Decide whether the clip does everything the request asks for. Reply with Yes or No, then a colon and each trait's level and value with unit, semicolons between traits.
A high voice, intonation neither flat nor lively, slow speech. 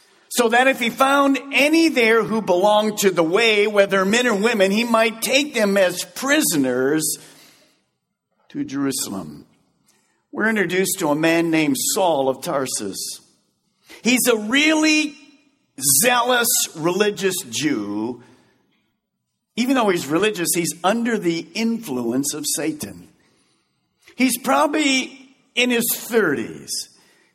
No: high, 215 Hz; wide, 7.5 semitones; slow, 120 wpm